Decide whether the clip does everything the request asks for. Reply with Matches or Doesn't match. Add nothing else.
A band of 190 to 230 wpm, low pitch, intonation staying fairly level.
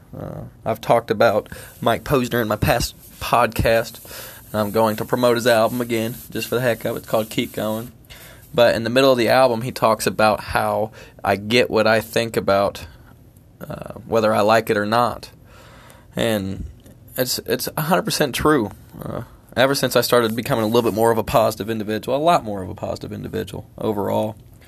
Matches